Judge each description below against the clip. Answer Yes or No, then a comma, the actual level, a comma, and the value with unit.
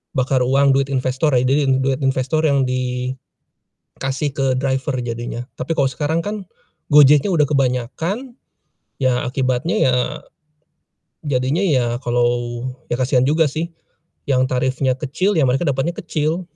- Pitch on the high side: No, low, 135 Hz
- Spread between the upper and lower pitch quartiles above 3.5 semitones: No, average, 3.0 semitones